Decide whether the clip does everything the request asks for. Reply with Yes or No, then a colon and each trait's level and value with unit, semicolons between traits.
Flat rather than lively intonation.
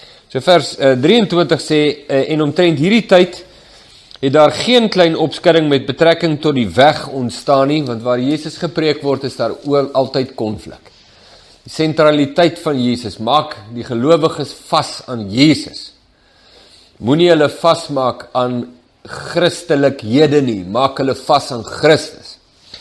No: average, 4.0 semitones